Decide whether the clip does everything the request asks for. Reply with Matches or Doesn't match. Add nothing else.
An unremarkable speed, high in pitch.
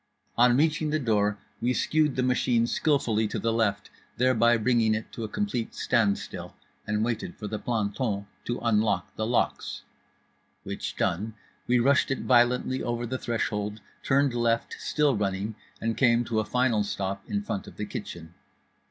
Doesn't match